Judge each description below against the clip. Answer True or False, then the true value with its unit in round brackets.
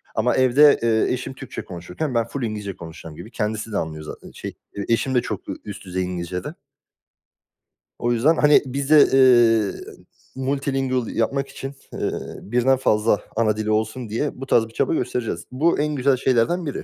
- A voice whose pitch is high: False (120 Hz)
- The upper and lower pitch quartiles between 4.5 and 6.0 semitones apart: False (3.9 semitones)